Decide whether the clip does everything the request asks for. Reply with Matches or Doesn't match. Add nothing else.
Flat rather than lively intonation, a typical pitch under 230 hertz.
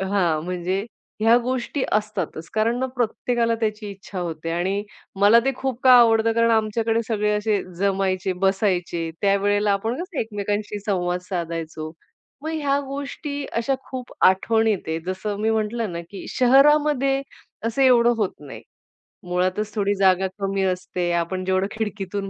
Doesn't match